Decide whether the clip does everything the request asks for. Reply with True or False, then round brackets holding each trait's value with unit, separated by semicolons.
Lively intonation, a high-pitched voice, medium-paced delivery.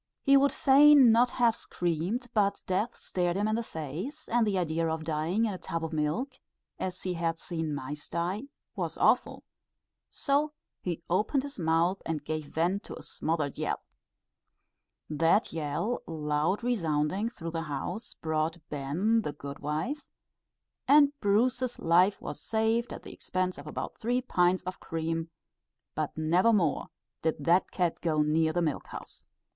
False (6.0 semitones; 175 Hz; 160 wpm)